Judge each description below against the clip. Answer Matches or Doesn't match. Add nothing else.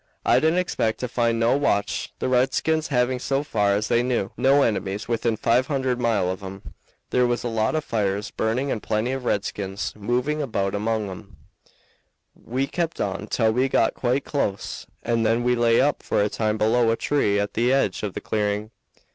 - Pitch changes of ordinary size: Matches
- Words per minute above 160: Matches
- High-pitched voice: Doesn't match